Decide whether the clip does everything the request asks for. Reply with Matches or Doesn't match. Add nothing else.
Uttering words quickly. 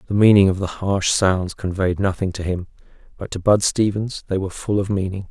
Matches